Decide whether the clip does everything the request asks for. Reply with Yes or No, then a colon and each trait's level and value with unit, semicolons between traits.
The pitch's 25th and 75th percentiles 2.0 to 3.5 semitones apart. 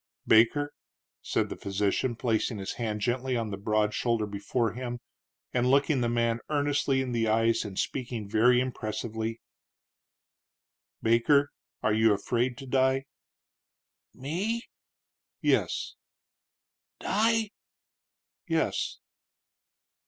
Yes: average, 3.2 semitones